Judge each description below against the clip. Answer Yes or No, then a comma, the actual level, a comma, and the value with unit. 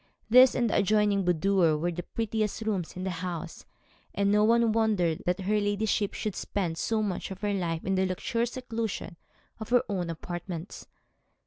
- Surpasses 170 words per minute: Yes, average, 180 wpm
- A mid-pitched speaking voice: No, high, 200 Hz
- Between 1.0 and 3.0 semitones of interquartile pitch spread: No, average, 3.5 semitones